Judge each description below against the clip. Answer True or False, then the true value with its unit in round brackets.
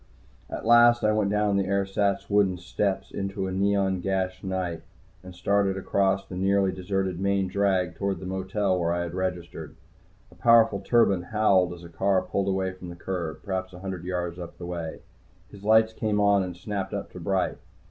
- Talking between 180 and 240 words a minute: True (190 wpm)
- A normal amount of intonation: False (1.6 semitones)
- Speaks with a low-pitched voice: True (95 Hz)